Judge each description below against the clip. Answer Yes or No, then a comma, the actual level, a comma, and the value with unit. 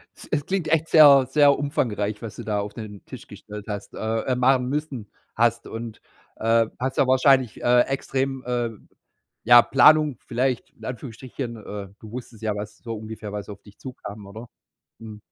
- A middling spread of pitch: Yes, average, 3.7 semitones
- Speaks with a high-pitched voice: No, low, 120 Hz